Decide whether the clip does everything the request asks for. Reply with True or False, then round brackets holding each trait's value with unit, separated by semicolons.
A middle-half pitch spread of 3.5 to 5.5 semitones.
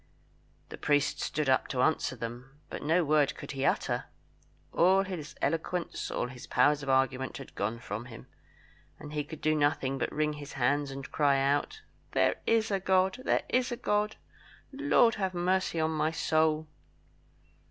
True (4.9 semitones)